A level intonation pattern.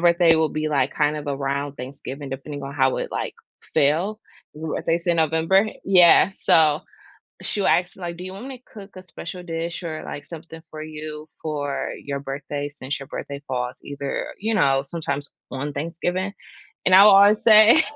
No: average, 4.1 semitones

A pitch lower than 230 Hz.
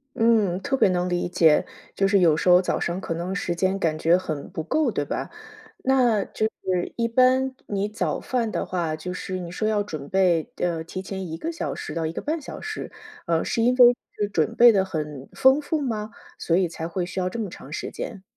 Yes: high, 190 Hz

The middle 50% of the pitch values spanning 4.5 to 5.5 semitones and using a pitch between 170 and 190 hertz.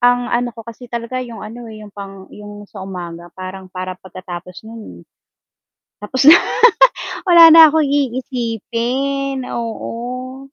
No: average, 4.8 semitones; high, 230 Hz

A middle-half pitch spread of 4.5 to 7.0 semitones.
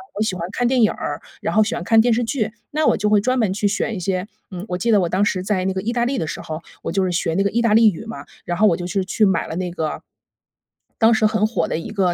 No: average, 3.6 semitones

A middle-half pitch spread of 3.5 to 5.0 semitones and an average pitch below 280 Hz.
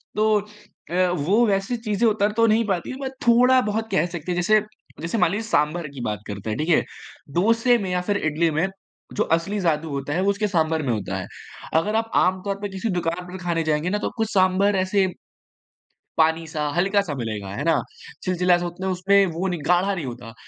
Yes: average, 4.1 semitones; medium, 185 Hz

